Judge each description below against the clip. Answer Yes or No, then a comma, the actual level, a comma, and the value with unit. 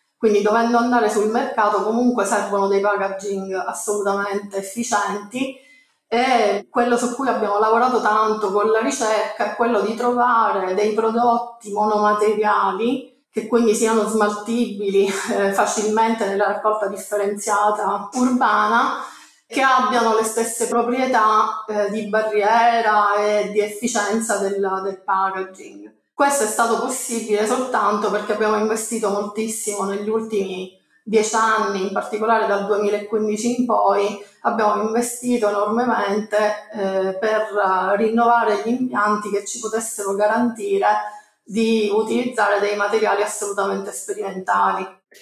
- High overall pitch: Yes, high, 215 Hz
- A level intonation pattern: Yes, narrow, 2.0 semitones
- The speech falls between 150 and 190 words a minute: No, average, 120 wpm